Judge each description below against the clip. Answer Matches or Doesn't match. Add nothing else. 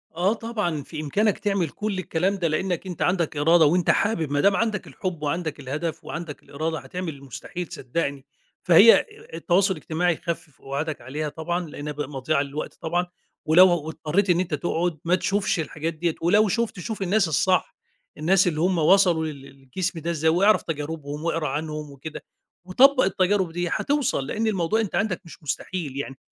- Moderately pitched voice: Matches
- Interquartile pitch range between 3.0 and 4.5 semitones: Matches